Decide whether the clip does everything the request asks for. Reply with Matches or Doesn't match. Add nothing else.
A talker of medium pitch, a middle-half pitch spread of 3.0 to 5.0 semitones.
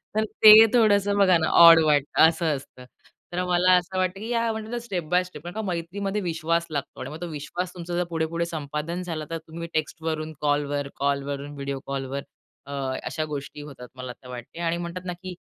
Matches